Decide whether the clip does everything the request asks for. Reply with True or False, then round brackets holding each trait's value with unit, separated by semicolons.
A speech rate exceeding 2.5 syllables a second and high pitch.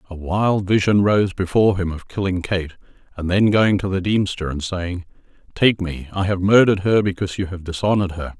False (5.6 syllables/s; 95 Hz)